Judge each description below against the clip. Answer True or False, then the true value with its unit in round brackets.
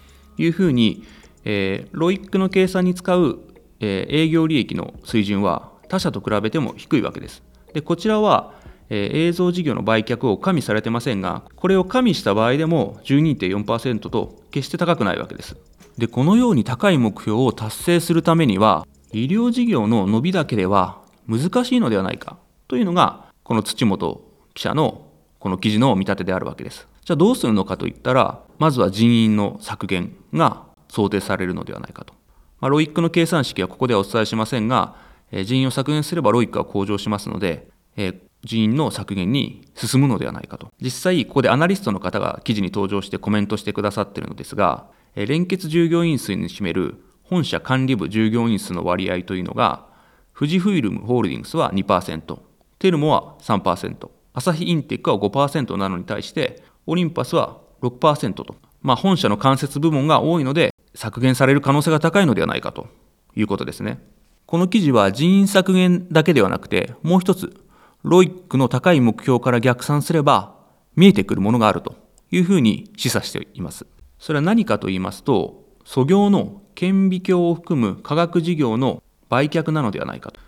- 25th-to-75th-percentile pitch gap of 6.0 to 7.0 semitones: False (8.8 semitones)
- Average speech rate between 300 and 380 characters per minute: True (360 characters per minute)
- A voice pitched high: False (135 Hz)